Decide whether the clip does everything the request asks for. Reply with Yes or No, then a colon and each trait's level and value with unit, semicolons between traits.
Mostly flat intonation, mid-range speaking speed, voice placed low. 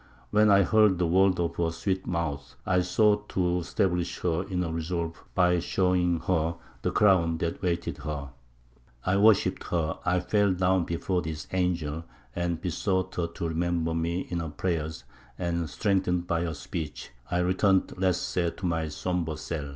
Yes: narrow, 2.0 semitones; average, 170 wpm; very low, 85 Hz